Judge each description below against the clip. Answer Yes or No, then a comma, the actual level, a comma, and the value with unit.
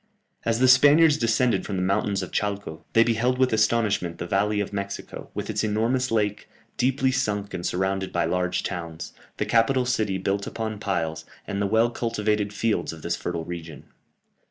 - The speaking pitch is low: Yes, low, 105 Hz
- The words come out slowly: No, average, 180 wpm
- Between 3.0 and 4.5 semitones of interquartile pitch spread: Yes, average, 3.4 semitones